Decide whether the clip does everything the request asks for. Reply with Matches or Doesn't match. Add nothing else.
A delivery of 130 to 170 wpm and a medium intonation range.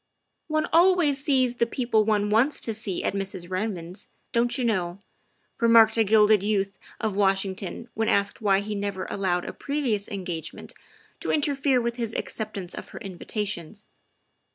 Matches